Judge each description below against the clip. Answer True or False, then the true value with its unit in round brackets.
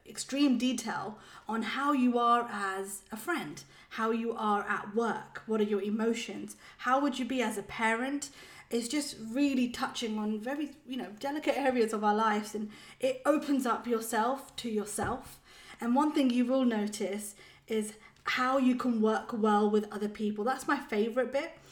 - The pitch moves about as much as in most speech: True (3.6 semitones)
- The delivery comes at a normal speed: True (175 wpm)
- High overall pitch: True (230 Hz)